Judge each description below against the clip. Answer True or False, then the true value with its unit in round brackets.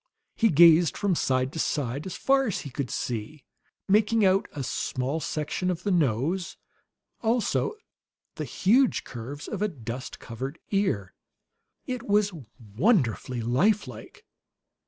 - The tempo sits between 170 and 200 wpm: False (135 wpm)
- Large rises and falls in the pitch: True (8.0 semitones)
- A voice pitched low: False (160 Hz)